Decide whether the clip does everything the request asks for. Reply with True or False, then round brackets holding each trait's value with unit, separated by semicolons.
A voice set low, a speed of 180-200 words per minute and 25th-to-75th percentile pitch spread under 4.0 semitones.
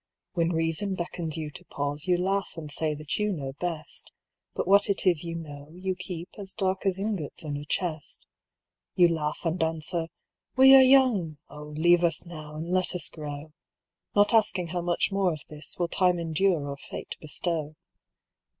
False (170 Hz; 185 wpm; 3.5 semitones)